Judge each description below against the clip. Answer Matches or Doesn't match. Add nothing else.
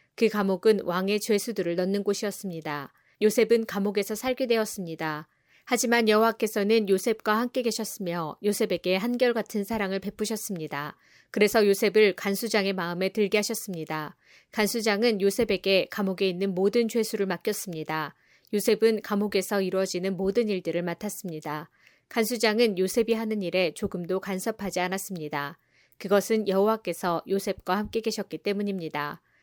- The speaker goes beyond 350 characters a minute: Matches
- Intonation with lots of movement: Doesn't match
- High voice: Matches